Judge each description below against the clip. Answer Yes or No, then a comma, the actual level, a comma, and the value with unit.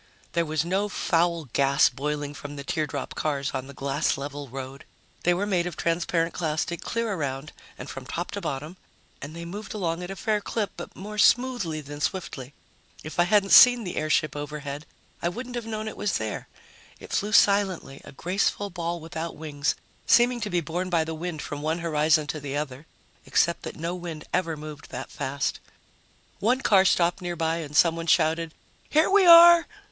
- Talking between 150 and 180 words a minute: No, average, 190 wpm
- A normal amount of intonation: Yes, average, 4.4 semitones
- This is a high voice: No, medium, 165 Hz